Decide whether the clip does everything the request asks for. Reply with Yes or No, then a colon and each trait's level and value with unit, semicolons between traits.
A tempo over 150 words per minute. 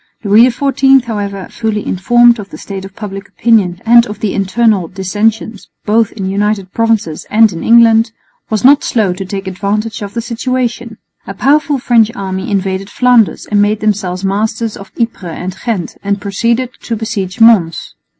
Yes: average, 170 wpm